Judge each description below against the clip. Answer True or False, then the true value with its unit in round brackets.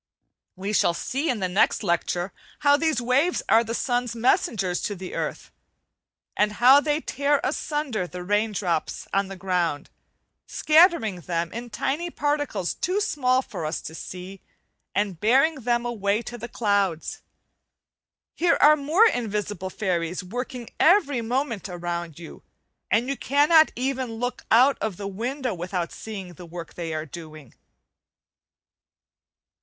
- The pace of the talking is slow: False (145 wpm)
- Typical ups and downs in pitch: False (6.7 semitones)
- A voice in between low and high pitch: False (220 Hz)